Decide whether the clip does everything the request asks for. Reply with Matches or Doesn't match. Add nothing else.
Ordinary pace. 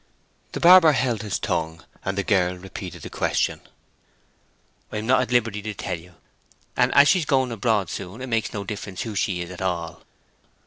Matches